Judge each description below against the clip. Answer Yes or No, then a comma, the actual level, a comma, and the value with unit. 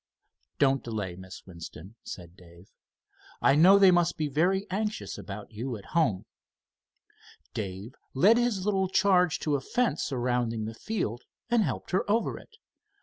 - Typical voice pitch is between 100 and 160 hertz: Yes, low, 135 Hz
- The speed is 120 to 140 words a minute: No, average, 150 wpm